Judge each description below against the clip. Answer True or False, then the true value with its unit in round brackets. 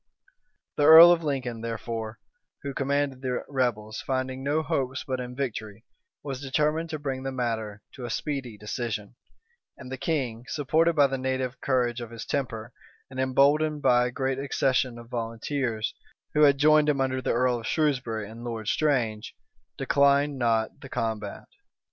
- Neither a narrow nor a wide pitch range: True (3.3 semitones)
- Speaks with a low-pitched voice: True (130 Hz)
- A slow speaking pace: False (165 wpm)